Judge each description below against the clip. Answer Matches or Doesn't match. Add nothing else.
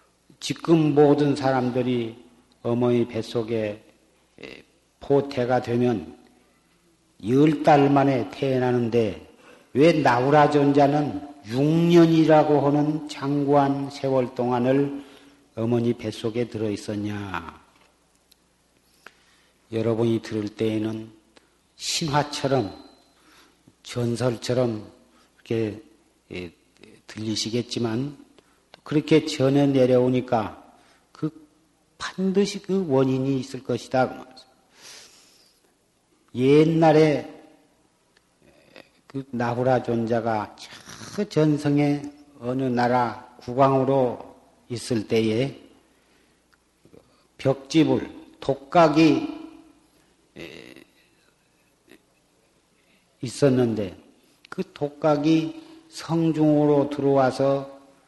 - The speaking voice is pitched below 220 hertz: Matches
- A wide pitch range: Doesn't match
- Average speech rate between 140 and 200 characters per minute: Matches